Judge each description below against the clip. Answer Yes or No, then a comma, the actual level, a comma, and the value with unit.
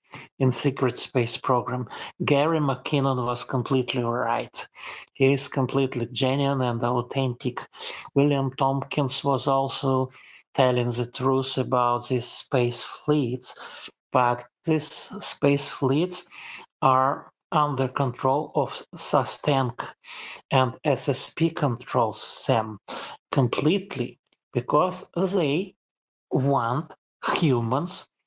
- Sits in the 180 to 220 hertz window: No, low, 135 Hz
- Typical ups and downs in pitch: No, narrow, 2.2 semitones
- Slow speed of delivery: Yes, slow, 95 wpm